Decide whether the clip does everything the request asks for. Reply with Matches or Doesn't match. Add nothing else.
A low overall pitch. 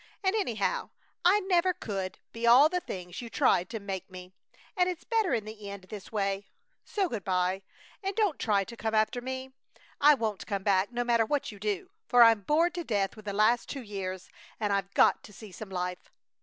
Doesn't match